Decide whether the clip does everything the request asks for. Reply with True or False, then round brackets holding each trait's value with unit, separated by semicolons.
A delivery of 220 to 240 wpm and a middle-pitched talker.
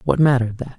False (230 wpm; 130 Hz)